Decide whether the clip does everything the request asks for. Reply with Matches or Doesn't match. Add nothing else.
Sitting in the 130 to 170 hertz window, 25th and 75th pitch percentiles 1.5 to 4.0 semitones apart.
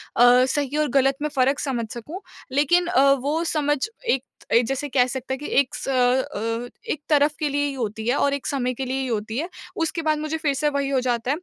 Doesn't match